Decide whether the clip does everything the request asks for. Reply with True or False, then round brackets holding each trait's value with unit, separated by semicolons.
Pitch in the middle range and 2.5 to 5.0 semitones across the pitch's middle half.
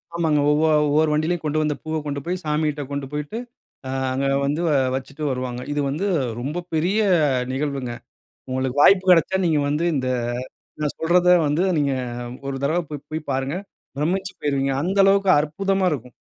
True (150 Hz; 3.5 semitones)